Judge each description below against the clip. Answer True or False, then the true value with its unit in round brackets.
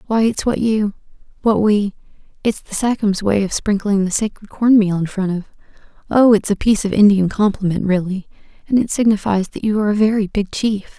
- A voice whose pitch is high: True (205 Hz)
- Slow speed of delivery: False (185 wpm)